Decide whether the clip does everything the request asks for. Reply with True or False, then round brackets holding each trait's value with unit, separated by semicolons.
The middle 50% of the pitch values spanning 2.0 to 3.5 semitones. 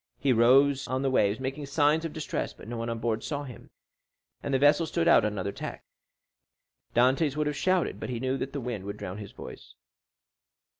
False (4.0 semitones)